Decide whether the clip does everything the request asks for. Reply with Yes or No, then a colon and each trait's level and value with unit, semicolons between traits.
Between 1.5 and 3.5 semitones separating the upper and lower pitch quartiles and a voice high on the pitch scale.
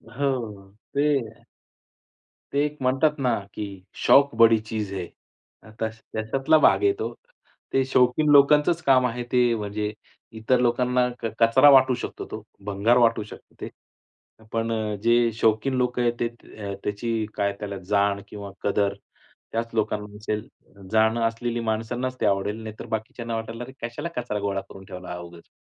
No: average, 3.2 semitones; low, 115 Hz